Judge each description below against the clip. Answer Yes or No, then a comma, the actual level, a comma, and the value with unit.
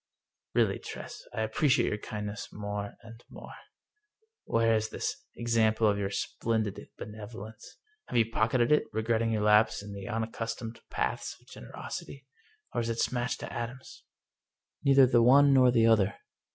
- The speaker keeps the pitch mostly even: Yes, narrow, 1.8 semitones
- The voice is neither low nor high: No, low, 115 Hz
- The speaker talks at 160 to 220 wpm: Yes, average, 165 wpm